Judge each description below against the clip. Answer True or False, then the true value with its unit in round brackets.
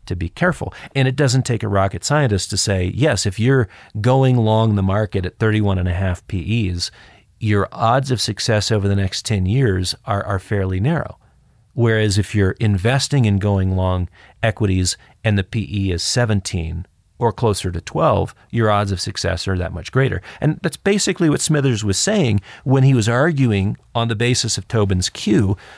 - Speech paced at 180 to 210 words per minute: True (185 wpm)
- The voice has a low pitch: True (105 Hz)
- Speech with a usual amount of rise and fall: True (4.0 semitones)